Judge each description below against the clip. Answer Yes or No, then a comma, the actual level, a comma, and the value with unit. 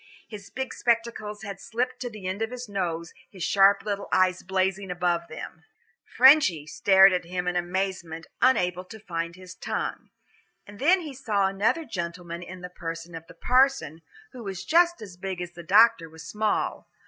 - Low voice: No, high, 190 Hz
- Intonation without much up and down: No, average, 4.1 semitones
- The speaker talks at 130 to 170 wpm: No, average, 180 wpm